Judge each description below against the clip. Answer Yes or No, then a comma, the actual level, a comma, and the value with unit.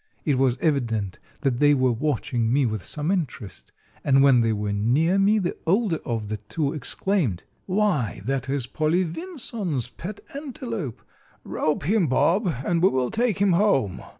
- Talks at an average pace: Yes, average, 165 wpm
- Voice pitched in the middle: Yes, medium, 145 Hz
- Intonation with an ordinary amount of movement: No, wide, 7.6 semitones